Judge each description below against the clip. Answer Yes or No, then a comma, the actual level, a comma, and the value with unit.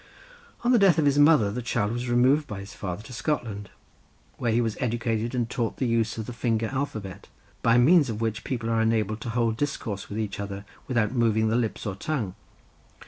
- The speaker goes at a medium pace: No, fast, 210 wpm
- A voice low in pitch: Yes, low, 115 Hz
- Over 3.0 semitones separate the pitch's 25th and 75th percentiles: No, average, 2.7 semitones